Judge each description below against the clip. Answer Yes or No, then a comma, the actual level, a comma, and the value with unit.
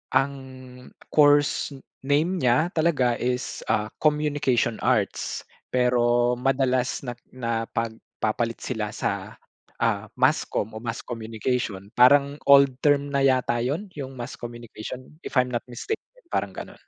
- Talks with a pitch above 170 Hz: No, low, 125 Hz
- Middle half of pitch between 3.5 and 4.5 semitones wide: No, average, 3.0 semitones